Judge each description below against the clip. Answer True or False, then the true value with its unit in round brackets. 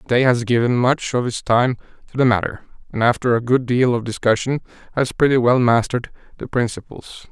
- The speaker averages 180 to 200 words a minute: True (190 wpm)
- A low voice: True (120 Hz)